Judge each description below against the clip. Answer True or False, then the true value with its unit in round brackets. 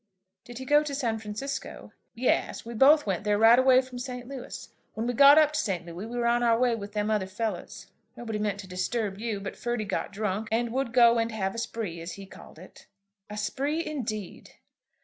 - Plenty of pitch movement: False (3.2 semitones)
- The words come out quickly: True (220 wpm)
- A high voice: True (230 Hz)